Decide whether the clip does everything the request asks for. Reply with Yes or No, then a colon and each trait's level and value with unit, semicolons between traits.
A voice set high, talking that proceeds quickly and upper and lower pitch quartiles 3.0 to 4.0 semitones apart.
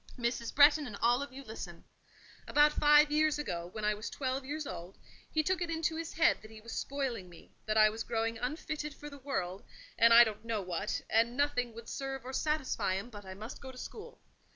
No: high, 245 Hz; fast, 225 wpm; average, 5.3 semitones